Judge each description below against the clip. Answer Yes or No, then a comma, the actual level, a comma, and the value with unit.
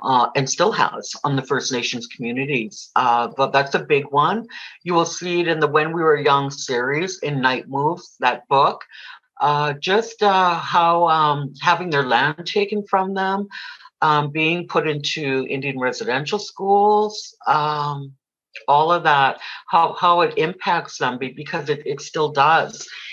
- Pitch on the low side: No, medium, 155 Hz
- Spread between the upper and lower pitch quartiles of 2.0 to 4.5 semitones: No, average, 4.9 semitones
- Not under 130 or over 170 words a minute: Yes, average, 165 wpm